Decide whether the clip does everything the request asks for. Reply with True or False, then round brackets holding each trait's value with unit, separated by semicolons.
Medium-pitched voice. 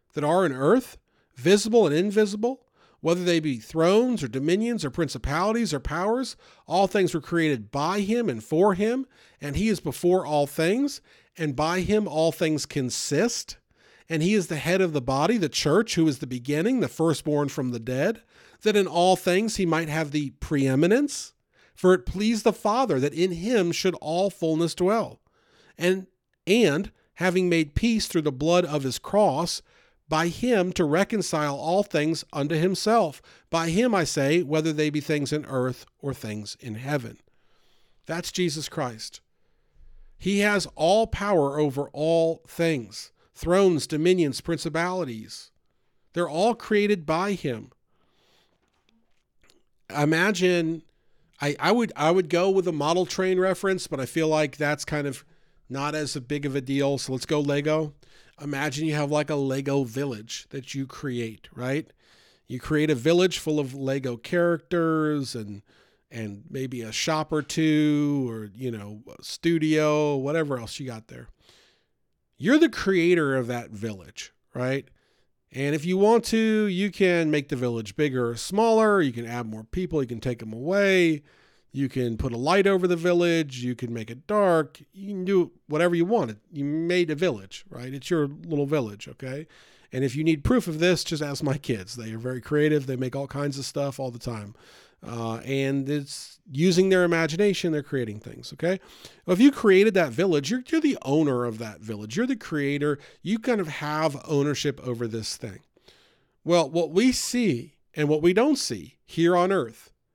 True (155 Hz)